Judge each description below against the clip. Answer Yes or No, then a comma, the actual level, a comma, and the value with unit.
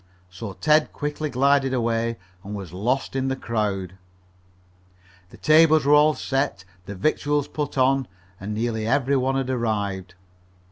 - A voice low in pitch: Yes, low, 130 Hz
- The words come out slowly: No, average, 145 wpm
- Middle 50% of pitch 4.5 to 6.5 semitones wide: Yes, average, 5.1 semitones